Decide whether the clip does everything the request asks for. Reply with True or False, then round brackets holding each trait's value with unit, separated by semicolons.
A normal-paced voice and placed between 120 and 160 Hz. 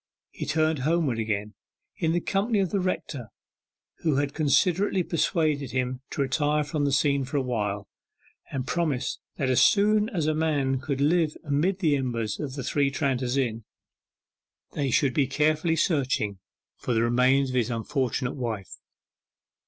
True (160 wpm; 140 Hz)